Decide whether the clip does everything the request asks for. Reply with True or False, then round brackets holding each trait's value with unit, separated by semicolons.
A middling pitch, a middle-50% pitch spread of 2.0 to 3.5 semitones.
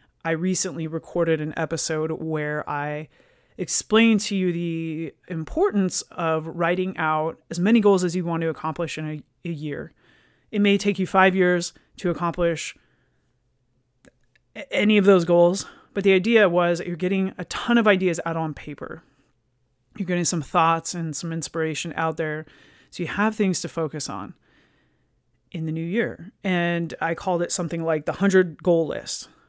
True (170 Hz; 2.7 semitones)